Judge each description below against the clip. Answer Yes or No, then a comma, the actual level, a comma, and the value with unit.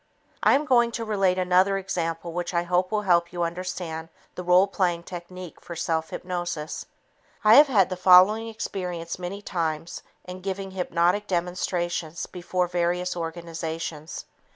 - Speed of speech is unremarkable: Yes, average, 150 wpm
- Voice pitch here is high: No, medium, 180 Hz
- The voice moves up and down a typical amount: No, narrow, 1.8 semitones